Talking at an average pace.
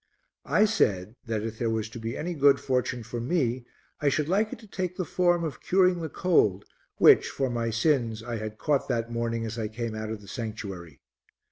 No: fast, 215 wpm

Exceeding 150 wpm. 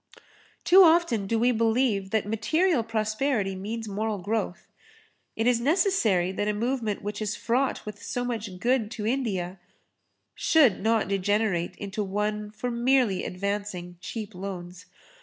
No: average, 140 wpm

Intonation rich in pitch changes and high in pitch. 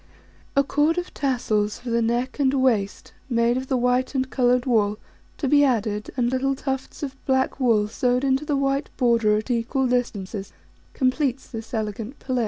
No: average, 2.8 semitones; very high, 250 Hz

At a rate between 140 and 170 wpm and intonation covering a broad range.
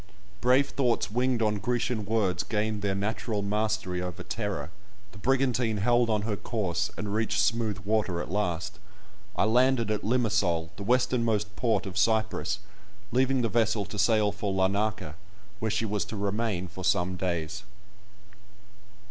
No: average, 150 wpm; narrow, 2.6 semitones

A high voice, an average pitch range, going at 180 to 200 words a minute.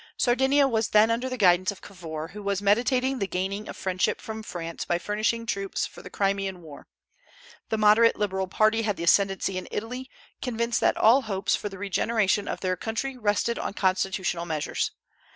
Yes: high, 205 Hz; average, 3.4 semitones; average, 185 wpm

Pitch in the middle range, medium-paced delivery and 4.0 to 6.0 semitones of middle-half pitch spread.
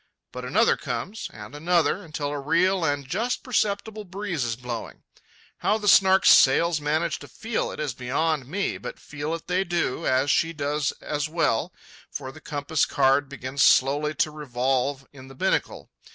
Yes: medium, 150 Hz; average, 170 wpm; average, 4.7 semitones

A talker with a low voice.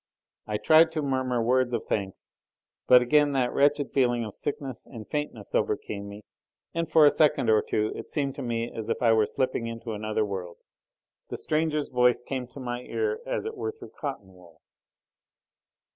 Yes: low, 125 Hz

